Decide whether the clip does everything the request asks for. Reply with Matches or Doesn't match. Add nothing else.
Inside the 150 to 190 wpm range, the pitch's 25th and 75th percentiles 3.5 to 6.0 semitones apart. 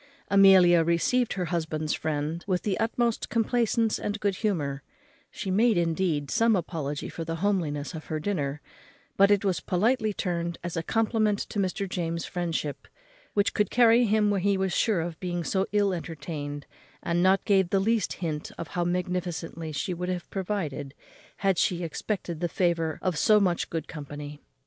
Matches